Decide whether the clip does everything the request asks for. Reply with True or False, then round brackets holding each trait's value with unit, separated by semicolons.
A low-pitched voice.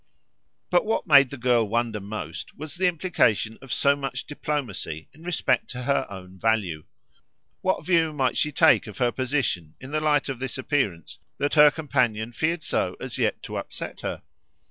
True (130 Hz)